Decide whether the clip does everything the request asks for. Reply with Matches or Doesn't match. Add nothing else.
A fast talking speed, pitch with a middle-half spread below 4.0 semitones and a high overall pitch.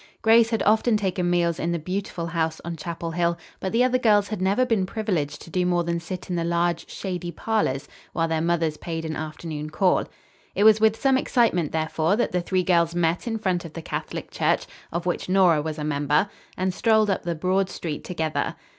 Doesn't match